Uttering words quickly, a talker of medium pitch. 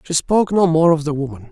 Yes: fast, 280 wpm; medium, 160 Hz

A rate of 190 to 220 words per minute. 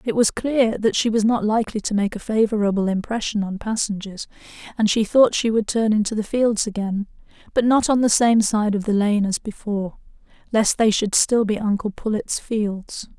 Yes: average, 200 wpm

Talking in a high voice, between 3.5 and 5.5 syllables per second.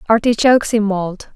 Yes: high, 215 Hz; 5.3 syllables/s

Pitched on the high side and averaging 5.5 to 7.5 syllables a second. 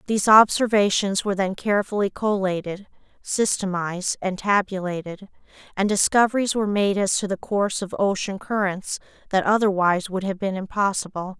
Yes: high, 195 Hz; 5.6 syllables/s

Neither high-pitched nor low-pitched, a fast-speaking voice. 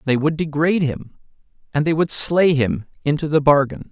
No: medium, 150 Hz; average, 185 wpm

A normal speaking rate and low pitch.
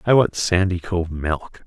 Yes: average, 145 wpm; very low, 90 Hz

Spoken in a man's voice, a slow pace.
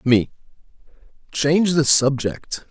Yes: male; slow, 90 wpm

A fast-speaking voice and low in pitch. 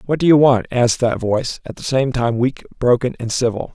Yes: fast, 240 wpm; low, 125 Hz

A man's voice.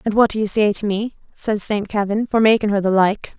No: female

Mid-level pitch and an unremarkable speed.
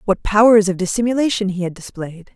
No: high, 200 Hz; average, 180 wpm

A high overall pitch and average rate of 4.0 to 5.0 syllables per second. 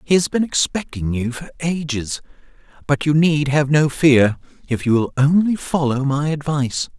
No: medium, 145 Hz; 4.7 syllables/s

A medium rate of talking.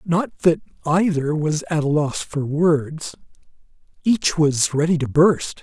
Yes: average, 150 wpm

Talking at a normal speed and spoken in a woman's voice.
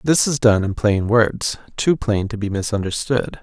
No: average, 175 wpm; male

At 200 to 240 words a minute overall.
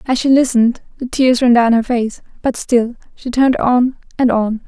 Yes: fast, 205 wpm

